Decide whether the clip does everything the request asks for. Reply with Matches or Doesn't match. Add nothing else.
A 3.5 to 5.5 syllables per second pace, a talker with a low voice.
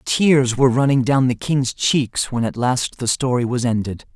Matches